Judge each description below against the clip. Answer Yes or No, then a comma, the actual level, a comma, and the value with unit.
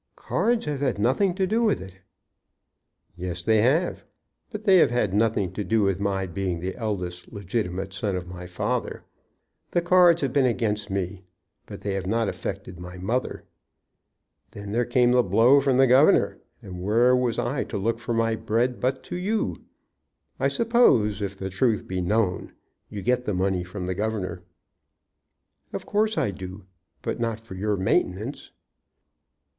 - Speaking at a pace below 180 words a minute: Yes, average, 170 wpm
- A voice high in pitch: No, low, 105 Hz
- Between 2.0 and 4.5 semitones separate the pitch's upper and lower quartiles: No, average, 5.0 semitones